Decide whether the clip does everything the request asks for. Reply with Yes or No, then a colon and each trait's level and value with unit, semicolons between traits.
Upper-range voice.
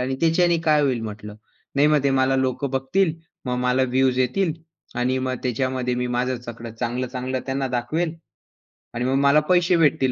No: low, 130 Hz